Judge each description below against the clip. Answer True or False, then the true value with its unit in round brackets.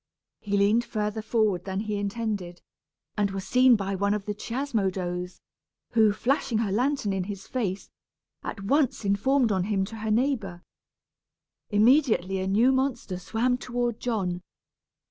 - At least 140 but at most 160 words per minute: True (145 wpm)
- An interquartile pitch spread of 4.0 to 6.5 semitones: False (3.6 semitones)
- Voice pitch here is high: True (210 Hz)